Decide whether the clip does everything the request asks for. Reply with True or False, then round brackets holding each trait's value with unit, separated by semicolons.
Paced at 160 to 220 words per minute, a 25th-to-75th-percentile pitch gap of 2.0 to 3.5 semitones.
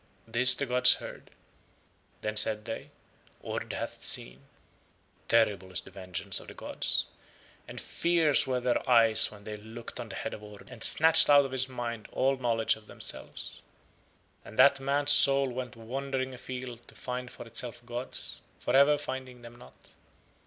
True (165 wpm; 2.9 semitones)